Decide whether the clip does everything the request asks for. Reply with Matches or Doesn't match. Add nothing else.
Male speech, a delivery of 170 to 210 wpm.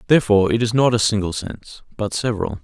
Matches